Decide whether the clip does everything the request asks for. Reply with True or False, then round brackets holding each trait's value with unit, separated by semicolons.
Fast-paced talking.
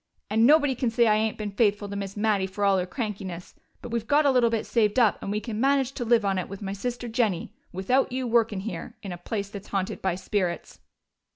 True (245 wpm)